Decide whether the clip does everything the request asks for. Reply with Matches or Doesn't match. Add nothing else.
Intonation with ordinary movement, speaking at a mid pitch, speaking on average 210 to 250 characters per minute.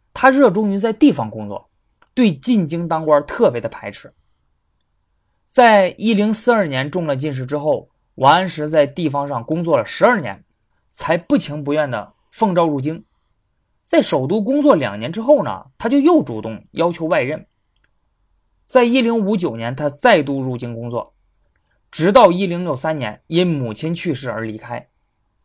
Doesn't match